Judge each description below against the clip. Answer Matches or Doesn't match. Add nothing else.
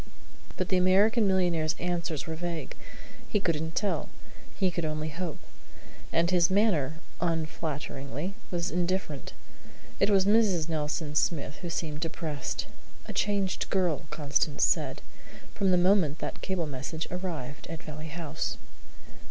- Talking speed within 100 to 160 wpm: Matches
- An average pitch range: Matches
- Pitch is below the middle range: Doesn't match